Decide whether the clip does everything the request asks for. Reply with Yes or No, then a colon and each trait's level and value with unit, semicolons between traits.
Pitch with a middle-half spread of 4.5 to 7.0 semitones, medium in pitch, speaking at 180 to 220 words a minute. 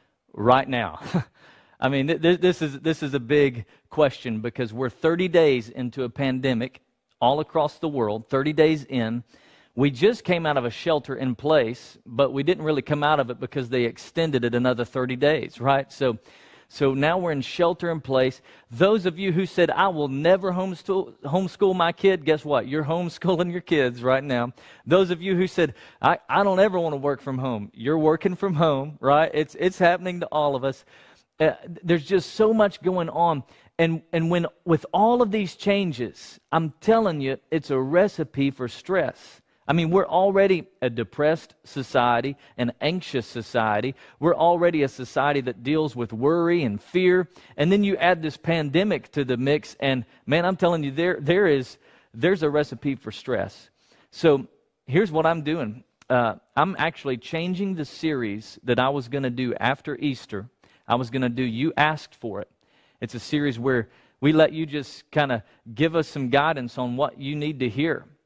Yes: average, 4.8 semitones; medium, 150 Hz; average, 190 wpm